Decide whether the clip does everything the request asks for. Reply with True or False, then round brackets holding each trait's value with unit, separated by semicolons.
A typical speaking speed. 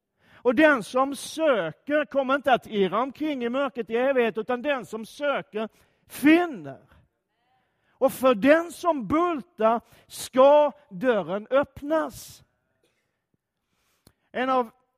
False (110 wpm)